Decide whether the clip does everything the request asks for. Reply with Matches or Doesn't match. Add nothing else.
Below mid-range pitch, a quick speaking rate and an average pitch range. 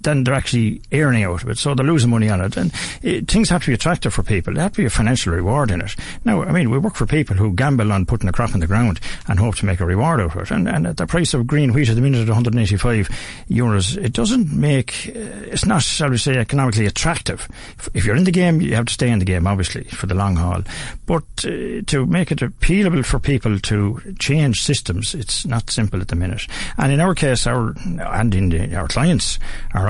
Doesn't match